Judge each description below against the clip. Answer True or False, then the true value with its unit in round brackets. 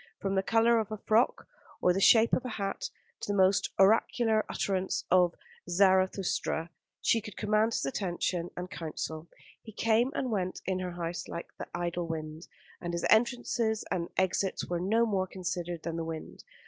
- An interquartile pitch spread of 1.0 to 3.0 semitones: False (4.0 semitones)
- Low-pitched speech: False (190 Hz)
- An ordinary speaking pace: True (175 wpm)